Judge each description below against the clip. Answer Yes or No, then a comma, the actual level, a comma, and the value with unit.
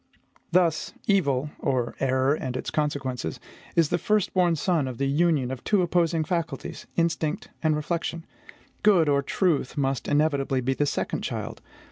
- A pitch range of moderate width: Yes, average, 3.9 semitones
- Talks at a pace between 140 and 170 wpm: Yes, average, 150 wpm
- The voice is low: No, medium, 150 Hz